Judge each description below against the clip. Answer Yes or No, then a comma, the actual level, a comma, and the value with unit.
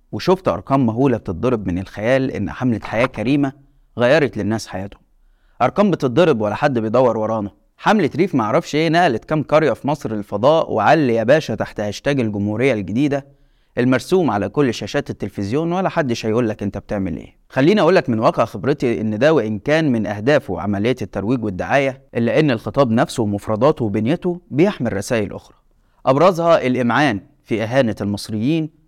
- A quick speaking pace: Yes, fast, 160 wpm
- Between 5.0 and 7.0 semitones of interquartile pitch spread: Yes, average, 5.3 semitones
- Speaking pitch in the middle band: No, low, 120 Hz